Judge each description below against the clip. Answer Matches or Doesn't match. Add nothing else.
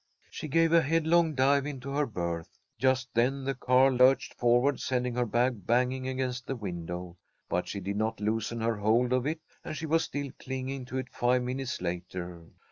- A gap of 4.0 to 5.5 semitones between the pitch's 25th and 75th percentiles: Doesn't match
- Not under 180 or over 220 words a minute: Matches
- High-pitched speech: Doesn't match